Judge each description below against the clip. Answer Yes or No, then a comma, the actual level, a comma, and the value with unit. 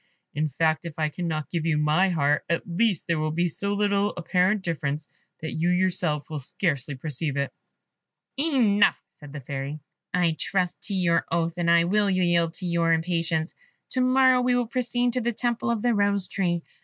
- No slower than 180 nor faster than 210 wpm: Yes, average, 190 wpm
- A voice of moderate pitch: Yes, medium, 175 Hz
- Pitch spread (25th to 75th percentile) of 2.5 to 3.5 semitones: No, average, 4.2 semitones